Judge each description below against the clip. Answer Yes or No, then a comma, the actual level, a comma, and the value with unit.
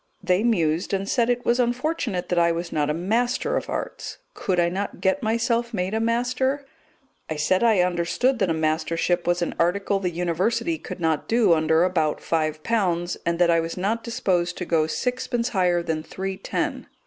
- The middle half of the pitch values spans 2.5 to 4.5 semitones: No, wide, 5.5 semitones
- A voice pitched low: No, medium, 185 Hz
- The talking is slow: No, average, 195 wpm